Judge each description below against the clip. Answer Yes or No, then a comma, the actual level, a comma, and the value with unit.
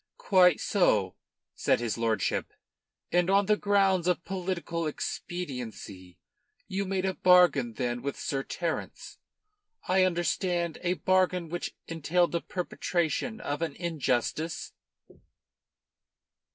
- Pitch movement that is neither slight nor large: Yes, average, 4.7 semitones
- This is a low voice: No, medium, 175 Hz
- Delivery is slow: Yes, slow, 110 wpm